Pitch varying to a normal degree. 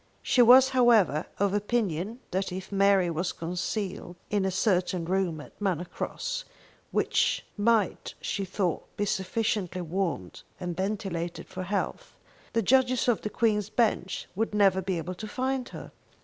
Yes: average, 3.6 semitones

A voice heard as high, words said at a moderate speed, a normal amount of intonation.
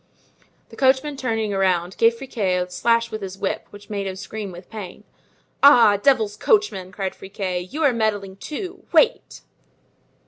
Yes: high, 210 Hz; average, 150 wpm; average, 4.7 semitones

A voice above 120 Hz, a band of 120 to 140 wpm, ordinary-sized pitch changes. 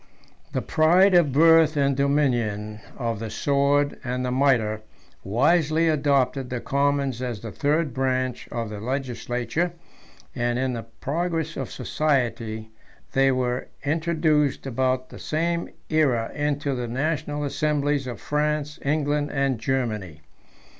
Yes: medium, 140 Hz; slow, 135 wpm; average, 3.4 semitones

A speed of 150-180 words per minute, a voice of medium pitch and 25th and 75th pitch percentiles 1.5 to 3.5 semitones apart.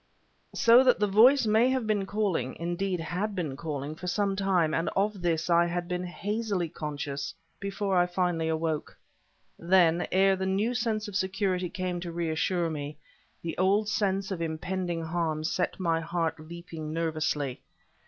Yes: average, 165 wpm; medium, 180 Hz; average, 3.2 semitones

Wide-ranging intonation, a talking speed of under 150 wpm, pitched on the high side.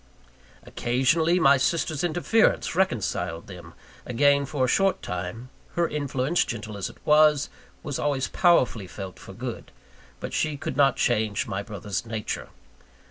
No: wide, 6.3 semitones; average, 140 wpm; low, 130 Hz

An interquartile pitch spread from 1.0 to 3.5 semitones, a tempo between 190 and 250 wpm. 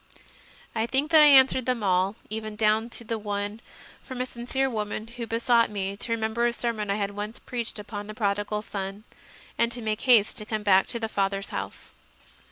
Yes: narrow, 2.5 semitones; average, 200 wpm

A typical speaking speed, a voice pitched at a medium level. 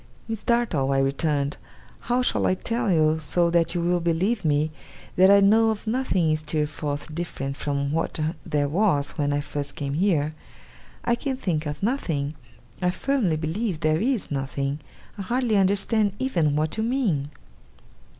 Yes: average, 165 wpm; medium, 165 Hz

